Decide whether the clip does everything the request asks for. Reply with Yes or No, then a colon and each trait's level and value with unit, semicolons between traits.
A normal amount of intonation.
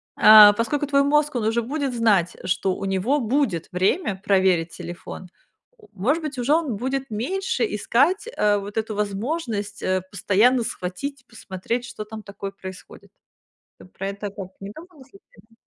No: wide, 6.0 semitones